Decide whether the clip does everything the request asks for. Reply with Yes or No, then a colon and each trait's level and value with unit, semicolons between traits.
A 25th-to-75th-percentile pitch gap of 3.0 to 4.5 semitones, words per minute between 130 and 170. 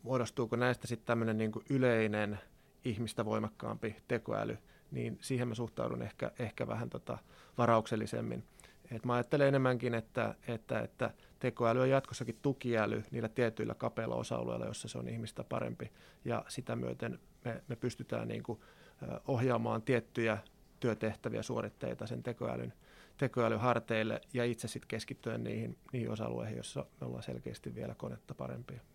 No: narrow, 2.4 semitones; average, 140 wpm